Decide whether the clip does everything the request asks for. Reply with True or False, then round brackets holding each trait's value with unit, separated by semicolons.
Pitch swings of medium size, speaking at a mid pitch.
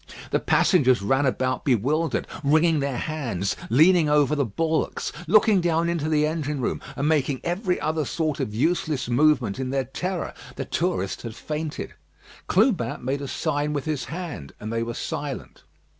True (3.9 semitones; 150 Hz)